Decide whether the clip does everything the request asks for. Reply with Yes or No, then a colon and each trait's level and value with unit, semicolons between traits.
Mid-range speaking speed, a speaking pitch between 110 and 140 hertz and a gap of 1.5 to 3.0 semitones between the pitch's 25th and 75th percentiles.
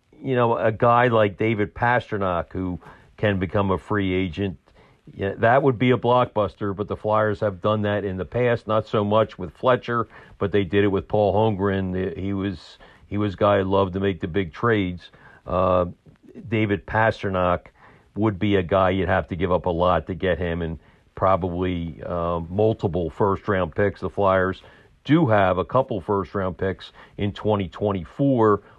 No: average, 180 wpm; low, 100 Hz; average, 2.7 semitones